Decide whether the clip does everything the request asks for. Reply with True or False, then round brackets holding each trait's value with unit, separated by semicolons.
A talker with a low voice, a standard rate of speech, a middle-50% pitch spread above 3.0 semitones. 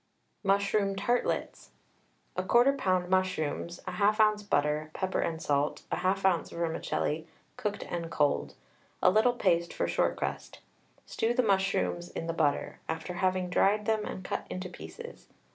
False (185 Hz; 145 wpm; 3.6 semitones)